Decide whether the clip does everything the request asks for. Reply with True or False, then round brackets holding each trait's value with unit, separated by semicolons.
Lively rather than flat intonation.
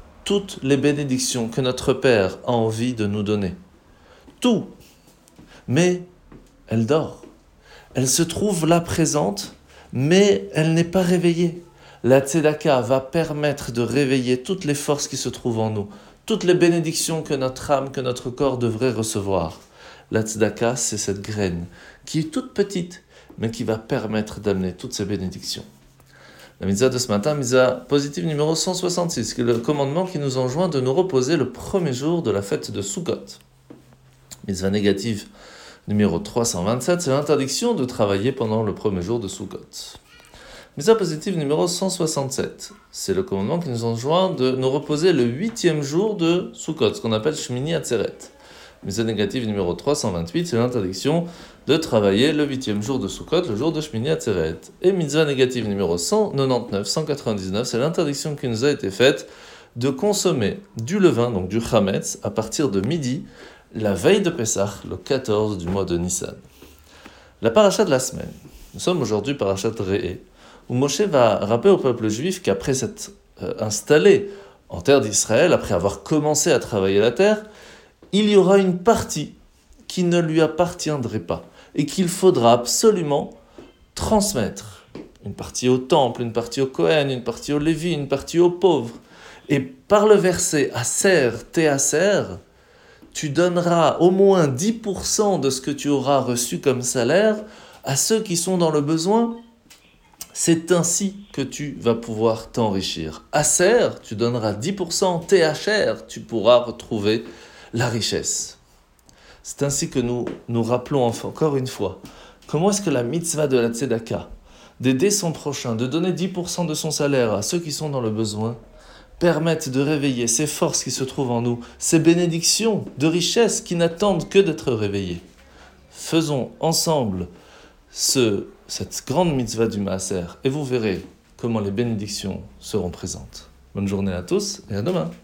True (7.1 semitones)